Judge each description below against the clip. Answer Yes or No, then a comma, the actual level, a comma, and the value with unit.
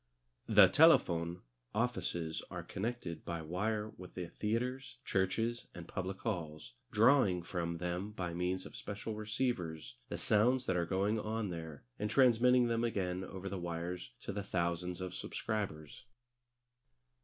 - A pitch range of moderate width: Yes, average, 4.2 semitones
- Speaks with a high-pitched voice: No, very low, 95 Hz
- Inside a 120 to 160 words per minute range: Yes, average, 145 wpm